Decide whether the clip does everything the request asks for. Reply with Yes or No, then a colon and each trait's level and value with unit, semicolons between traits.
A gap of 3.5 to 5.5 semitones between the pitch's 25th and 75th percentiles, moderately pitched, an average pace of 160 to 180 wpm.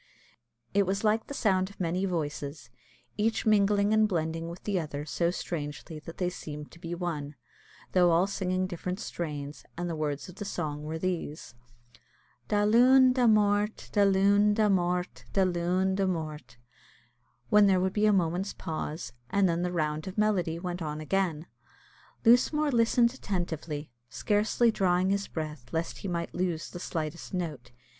Yes: average, 3.9 semitones; medium, 180 Hz; average, 165 wpm